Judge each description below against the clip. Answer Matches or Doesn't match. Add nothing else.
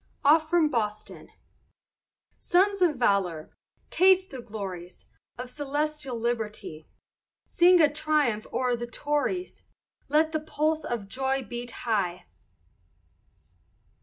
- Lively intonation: Matches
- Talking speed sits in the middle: Doesn't match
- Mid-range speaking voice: Doesn't match